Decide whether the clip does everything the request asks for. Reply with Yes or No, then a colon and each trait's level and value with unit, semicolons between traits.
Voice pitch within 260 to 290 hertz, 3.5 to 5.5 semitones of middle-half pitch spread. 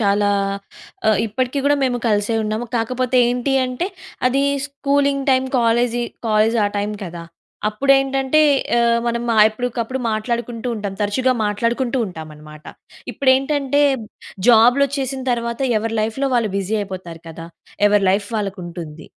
No: high, 235 Hz; average, 4.0 semitones